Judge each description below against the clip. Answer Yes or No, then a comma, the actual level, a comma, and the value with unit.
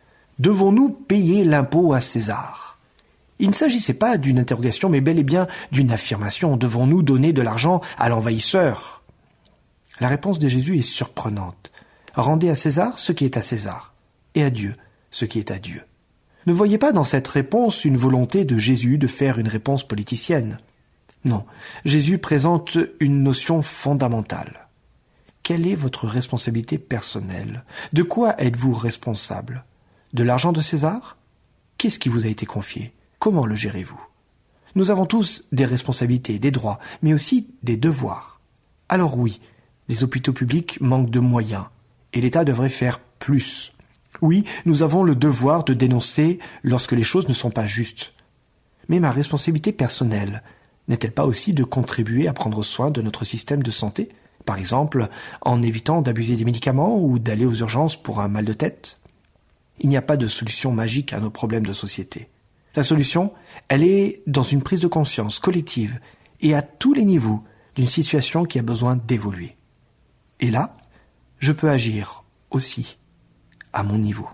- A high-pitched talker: No, low, 130 Hz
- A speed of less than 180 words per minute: Yes, average, 165 wpm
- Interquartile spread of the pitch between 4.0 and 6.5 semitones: Yes, wide, 5.5 semitones